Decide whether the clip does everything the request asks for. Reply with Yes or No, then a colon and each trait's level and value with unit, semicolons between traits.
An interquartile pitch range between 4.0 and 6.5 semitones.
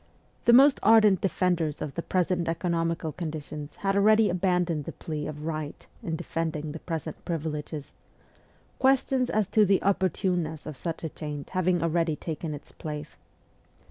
No: average, 3.3 semitones